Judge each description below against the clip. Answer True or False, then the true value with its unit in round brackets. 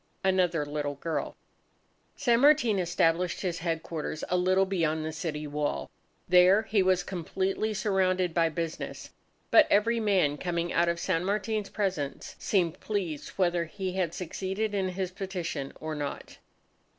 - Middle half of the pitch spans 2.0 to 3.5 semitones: True (2.9 semitones)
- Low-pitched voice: False (180 Hz)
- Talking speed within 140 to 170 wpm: True (145 wpm)